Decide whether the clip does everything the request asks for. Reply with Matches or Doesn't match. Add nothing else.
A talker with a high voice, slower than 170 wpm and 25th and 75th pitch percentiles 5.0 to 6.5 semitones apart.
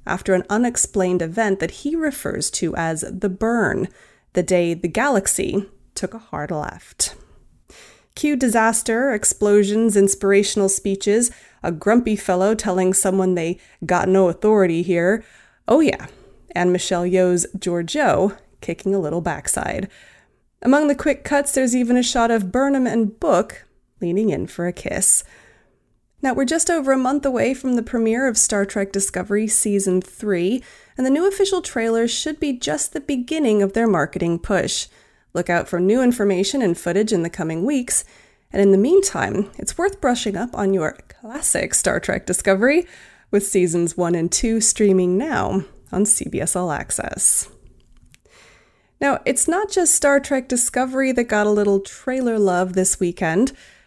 Matches